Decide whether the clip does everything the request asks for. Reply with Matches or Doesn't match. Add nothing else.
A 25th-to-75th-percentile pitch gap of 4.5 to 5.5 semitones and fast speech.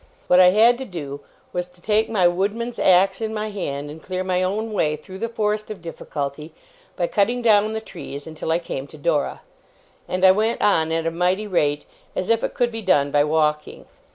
Matches